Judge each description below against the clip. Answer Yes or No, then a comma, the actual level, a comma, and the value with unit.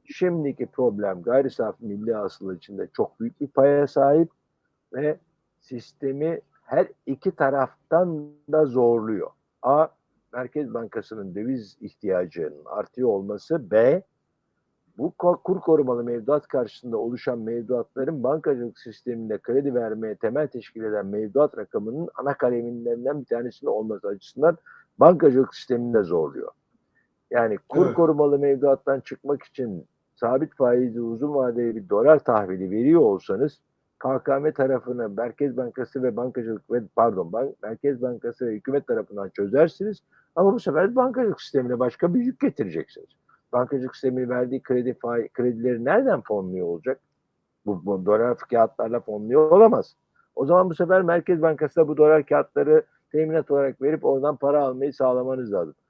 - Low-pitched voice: Yes, low, 130 Hz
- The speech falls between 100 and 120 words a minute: No, average, 130 wpm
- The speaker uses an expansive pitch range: No, average, 4.4 semitones